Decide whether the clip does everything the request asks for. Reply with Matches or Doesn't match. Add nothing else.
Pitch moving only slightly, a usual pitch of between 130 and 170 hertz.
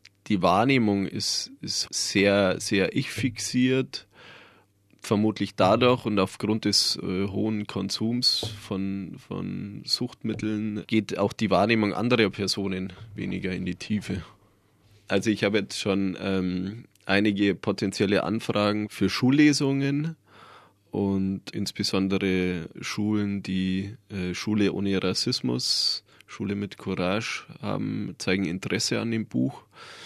Doesn't match